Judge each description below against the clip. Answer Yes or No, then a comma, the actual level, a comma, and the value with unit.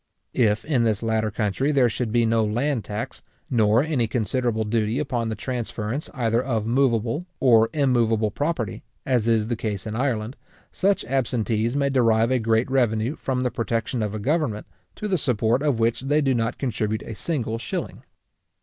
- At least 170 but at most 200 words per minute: Yes, average, 175 wpm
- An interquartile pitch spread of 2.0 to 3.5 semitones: Yes, average, 3.0 semitones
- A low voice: Yes, low, 115 Hz